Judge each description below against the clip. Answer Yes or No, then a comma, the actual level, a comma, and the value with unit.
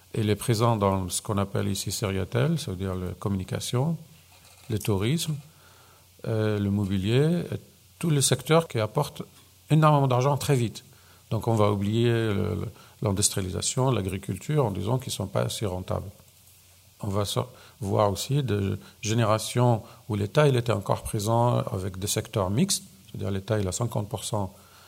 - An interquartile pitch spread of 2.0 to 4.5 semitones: Yes, average, 3.8 semitones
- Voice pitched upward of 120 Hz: No, low, 110 Hz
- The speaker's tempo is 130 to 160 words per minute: Yes, average, 150 wpm